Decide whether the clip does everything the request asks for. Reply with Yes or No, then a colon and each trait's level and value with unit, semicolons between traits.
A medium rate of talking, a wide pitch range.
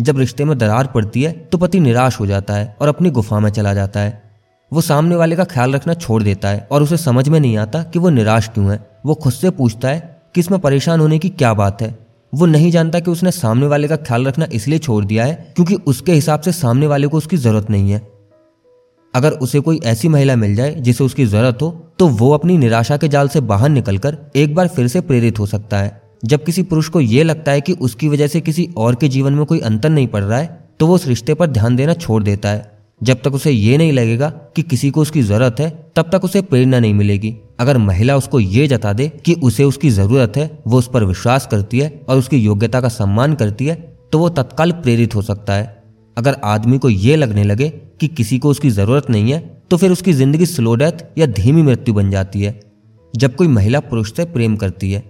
No: fast, 240 wpm; wide, 5.7 semitones